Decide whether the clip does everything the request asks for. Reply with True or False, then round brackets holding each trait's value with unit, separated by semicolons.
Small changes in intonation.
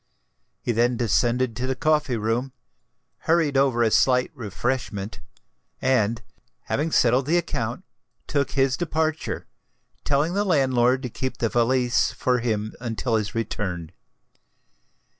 False (3.2 semitones)